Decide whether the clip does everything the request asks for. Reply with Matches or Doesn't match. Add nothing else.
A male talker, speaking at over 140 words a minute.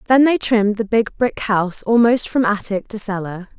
Doesn't match